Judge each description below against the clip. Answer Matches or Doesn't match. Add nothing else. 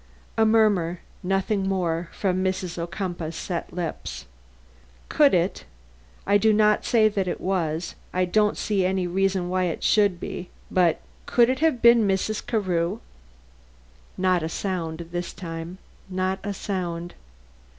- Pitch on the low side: Doesn't match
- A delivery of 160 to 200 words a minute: Doesn't match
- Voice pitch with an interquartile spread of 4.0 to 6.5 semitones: Doesn't match